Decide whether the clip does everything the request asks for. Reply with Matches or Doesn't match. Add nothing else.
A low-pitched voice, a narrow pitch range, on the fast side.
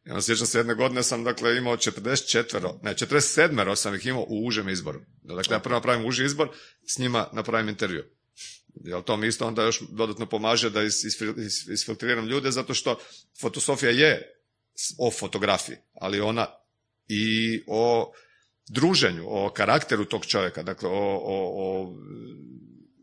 Doesn't match